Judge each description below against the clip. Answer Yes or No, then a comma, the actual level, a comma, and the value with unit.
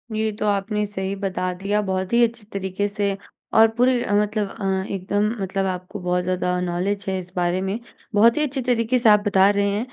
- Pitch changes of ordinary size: No, narrow, 2.1 semitones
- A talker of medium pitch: No, high, 200 Hz